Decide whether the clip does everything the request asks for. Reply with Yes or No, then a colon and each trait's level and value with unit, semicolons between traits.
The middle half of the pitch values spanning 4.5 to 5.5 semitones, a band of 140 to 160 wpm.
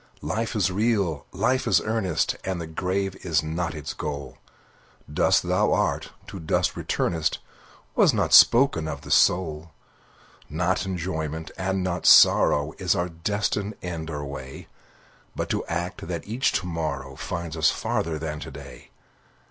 No: average, 3.4 semitones; average, 150 wpm